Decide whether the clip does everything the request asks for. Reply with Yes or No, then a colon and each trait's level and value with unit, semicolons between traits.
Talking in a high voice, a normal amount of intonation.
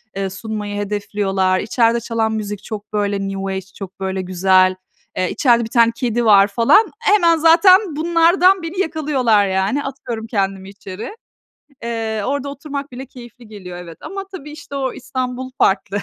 No: high, 225 Hz; wide, 6.1 semitones